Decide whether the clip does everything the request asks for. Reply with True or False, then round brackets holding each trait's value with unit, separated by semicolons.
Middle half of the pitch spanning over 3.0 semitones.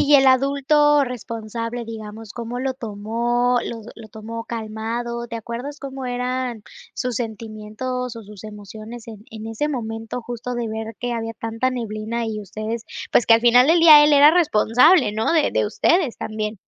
False (2.4 semitones)